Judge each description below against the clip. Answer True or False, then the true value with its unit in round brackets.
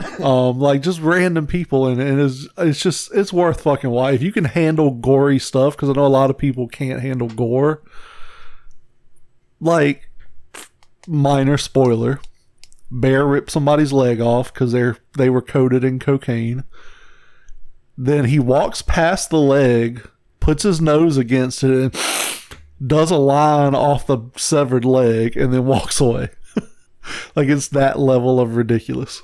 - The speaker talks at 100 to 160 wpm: True (155 wpm)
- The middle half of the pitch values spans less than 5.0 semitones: True (2.9 semitones)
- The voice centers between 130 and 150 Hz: True (135 Hz)